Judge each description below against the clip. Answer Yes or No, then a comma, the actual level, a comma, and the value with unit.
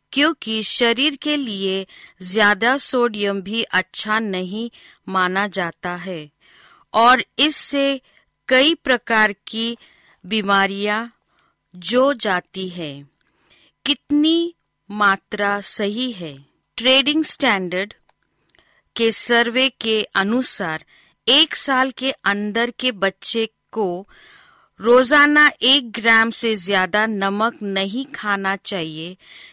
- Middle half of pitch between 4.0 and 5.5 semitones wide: Yes, average, 4.6 semitones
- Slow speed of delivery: Yes, slow, 95 wpm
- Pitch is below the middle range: No, high, 220 Hz